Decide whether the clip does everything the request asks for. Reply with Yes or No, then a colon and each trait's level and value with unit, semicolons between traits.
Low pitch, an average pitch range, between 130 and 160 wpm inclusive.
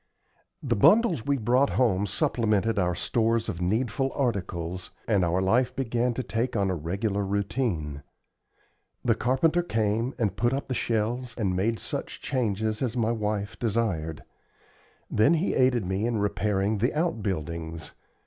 Yes: low, 110 Hz; average, 4.2 semitones; average, 150 wpm